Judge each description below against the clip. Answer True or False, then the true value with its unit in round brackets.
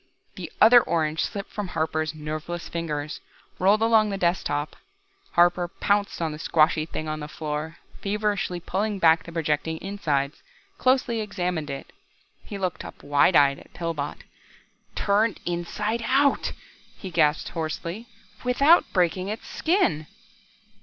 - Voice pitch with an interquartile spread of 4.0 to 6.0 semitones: True (4.9 semitones)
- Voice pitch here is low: False (175 Hz)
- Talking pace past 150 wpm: False (140 wpm)